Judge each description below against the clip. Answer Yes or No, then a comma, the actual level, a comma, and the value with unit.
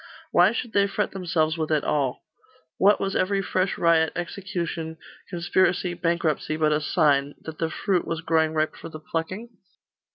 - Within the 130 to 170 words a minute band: Yes, average, 165 wpm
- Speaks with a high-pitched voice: No, medium, 165 Hz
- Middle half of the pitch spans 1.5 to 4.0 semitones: Yes, average, 3.0 semitones